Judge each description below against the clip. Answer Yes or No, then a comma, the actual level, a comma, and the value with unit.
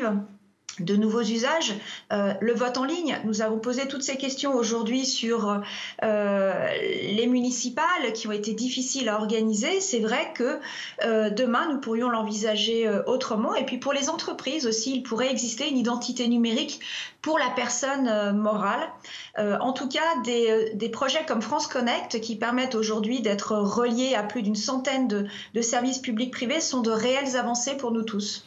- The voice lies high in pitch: Yes, high, 240 Hz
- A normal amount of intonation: Yes, average, 3.3 semitones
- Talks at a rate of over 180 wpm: No, average, 175 wpm